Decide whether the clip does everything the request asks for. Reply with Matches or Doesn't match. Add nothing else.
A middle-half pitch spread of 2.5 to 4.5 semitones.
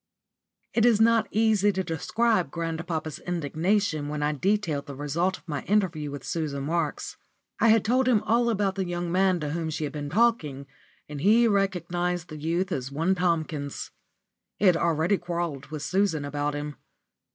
Doesn't match